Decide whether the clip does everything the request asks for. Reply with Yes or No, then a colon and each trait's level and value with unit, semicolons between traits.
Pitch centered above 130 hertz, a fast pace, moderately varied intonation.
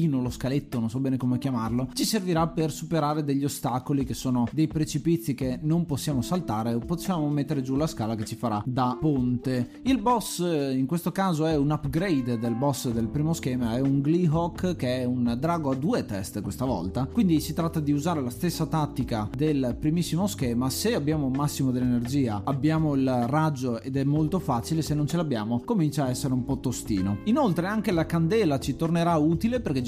Yes: medium, 140 Hz; fast, 195 wpm; average, 4.2 semitones